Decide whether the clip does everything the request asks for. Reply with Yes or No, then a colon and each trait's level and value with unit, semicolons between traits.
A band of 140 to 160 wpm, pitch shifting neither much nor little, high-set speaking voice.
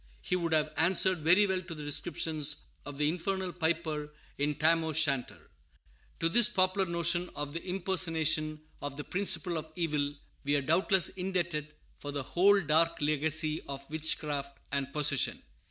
No: average, 155 wpm; average, 3.1 semitones; medium, 160 Hz